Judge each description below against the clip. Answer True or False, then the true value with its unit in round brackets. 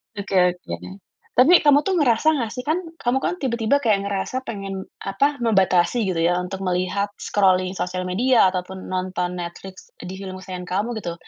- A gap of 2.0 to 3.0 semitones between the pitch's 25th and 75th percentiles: False (4.7 semitones)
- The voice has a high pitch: True (195 Hz)